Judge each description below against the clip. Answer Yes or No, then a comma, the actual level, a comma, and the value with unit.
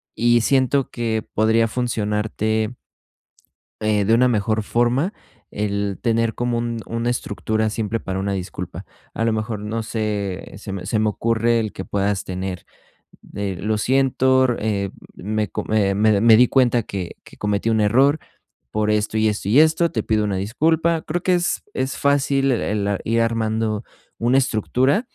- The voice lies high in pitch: No, low, 110 Hz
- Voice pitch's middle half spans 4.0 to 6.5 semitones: No, average, 2.7 semitones